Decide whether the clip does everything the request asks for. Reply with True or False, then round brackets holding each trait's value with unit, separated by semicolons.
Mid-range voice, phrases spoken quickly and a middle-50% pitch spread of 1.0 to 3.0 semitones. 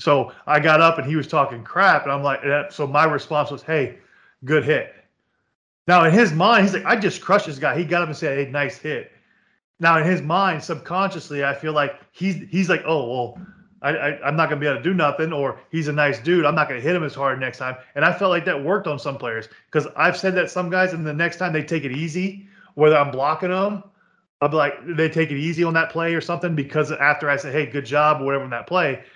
False (155 Hz; 265 wpm; 3.8 semitones)